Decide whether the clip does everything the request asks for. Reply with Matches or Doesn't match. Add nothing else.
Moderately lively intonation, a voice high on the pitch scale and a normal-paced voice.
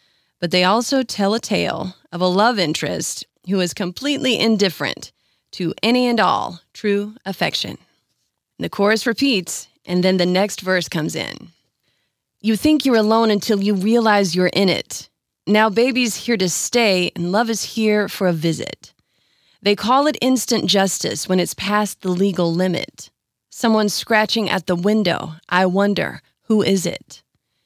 Matches